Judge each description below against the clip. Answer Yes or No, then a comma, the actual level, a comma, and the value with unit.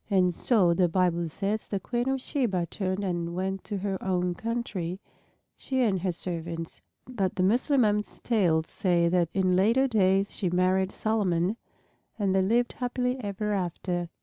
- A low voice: No, high, 190 Hz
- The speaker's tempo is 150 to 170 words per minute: Yes, average, 160 wpm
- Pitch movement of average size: Yes, average, 3.5 semitones